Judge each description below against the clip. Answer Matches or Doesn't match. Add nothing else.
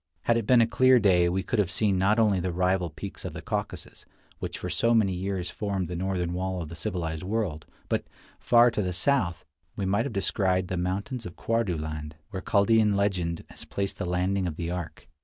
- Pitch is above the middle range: Doesn't match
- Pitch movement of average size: Matches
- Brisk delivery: Matches